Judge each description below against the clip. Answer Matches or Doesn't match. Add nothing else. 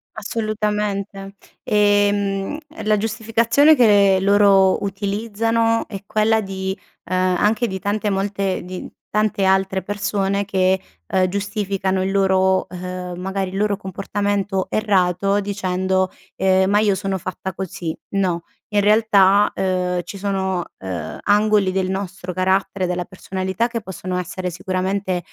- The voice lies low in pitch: Doesn't match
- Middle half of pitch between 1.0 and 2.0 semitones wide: Matches